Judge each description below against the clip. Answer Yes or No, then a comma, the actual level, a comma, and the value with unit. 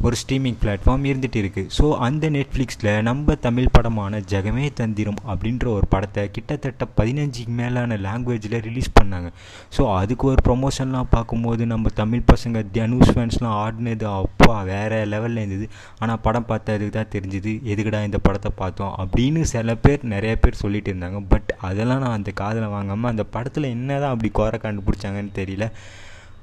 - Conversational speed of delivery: No, fast, 155 wpm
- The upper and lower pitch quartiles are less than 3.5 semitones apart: Yes, average, 3.0 semitones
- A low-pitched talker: Yes, low, 110 Hz